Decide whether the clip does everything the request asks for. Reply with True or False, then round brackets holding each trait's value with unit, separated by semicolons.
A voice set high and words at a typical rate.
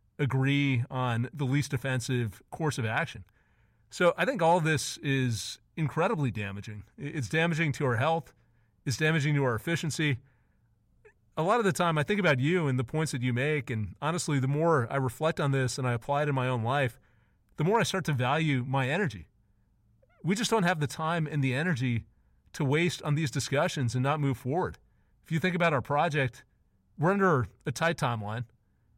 False (135 Hz; 195 wpm)